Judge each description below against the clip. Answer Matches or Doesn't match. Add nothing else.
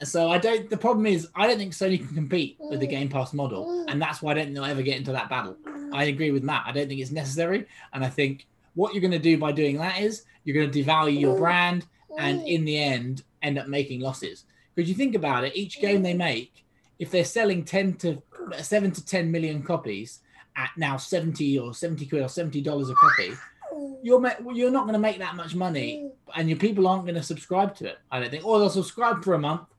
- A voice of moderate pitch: Matches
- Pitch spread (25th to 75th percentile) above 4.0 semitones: Matches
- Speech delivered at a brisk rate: Matches